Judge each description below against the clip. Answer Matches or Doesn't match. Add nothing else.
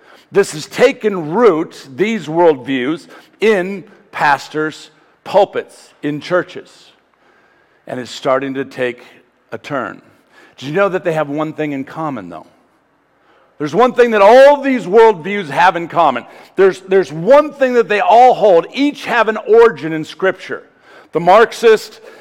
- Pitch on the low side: Doesn't match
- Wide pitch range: Matches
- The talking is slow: Doesn't match